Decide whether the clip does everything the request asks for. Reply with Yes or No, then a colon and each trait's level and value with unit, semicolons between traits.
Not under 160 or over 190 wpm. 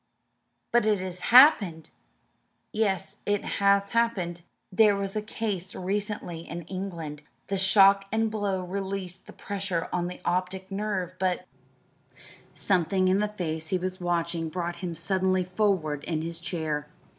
No: average, 145 wpm